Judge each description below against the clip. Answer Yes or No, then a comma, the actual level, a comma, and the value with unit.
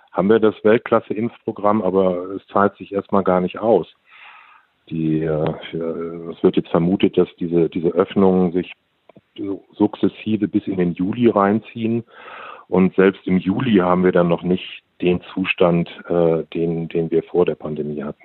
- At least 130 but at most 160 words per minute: Yes, average, 150 wpm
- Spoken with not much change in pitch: No, average, 3.1 semitones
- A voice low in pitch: Yes, very low, 90 Hz